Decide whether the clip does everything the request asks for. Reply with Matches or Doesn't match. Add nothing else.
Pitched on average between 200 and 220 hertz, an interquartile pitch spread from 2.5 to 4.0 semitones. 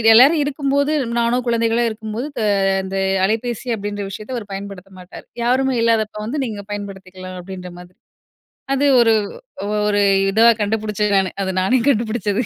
Matches